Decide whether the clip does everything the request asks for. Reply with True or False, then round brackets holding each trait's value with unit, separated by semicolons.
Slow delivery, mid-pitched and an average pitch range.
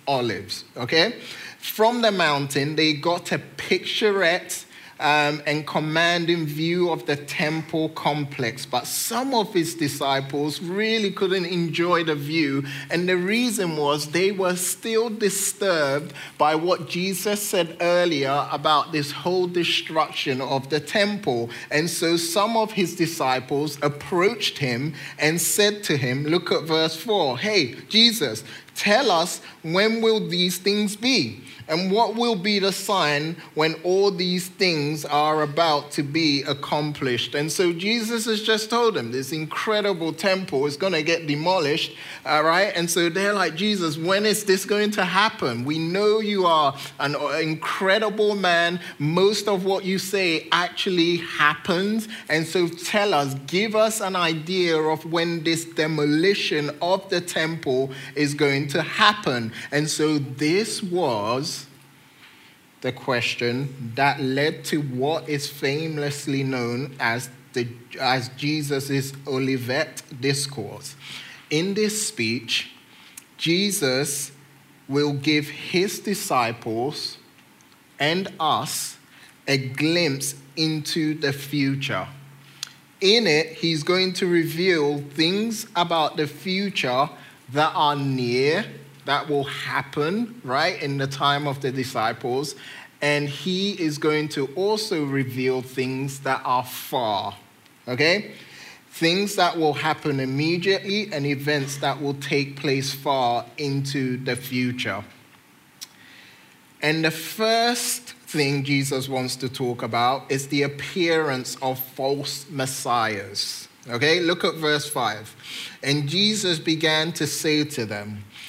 True (130 wpm; 155 Hz; 4.5 semitones)